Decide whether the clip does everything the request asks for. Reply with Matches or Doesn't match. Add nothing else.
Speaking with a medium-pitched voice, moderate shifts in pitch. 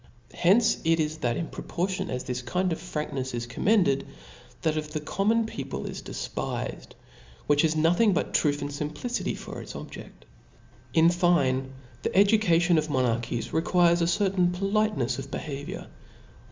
Matches